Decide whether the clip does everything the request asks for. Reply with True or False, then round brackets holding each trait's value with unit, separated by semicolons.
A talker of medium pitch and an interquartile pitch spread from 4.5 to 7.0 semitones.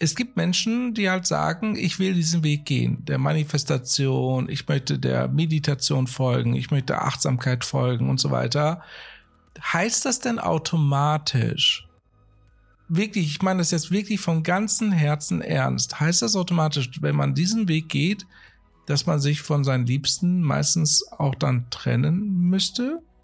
True (155 Hz; 5.1 semitones)